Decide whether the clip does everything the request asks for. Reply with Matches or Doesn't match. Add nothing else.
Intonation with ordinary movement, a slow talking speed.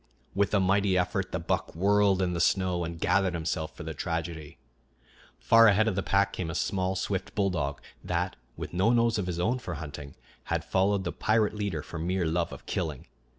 Doesn't match